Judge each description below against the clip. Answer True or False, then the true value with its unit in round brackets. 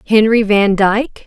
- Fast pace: False (140 wpm)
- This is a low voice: False (215 Hz)